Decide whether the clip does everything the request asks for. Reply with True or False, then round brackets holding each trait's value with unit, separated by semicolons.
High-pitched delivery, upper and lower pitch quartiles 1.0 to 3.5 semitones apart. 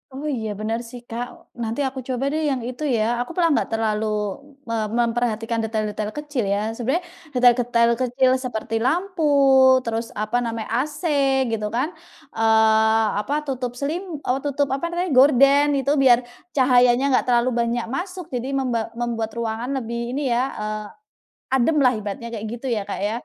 True (240 Hz; 3.2 semitones)